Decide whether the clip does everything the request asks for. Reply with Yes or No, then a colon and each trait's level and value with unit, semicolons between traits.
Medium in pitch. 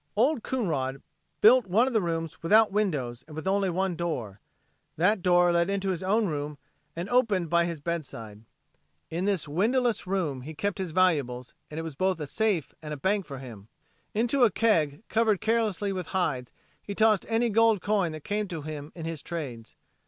Yes: medium, 180 Hz